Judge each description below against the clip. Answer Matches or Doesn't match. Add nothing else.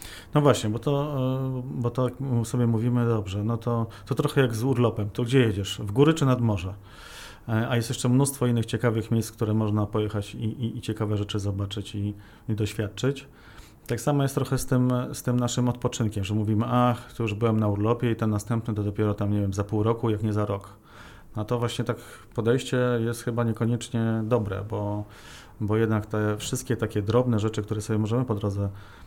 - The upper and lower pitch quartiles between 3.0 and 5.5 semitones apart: Doesn't match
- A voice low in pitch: Matches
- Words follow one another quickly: Matches